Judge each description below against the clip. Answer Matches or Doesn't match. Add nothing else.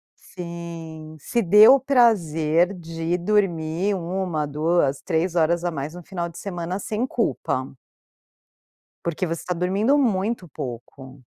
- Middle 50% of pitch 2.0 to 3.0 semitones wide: Doesn't match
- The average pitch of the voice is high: Doesn't match